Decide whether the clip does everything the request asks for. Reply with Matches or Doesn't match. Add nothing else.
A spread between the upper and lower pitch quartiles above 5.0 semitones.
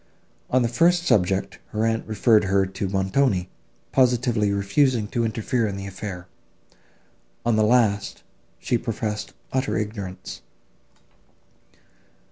Doesn't match